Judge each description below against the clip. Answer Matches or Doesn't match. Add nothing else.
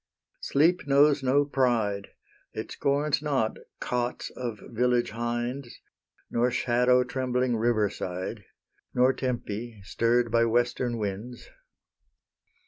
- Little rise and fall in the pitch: Matches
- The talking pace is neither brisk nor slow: Doesn't match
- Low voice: Matches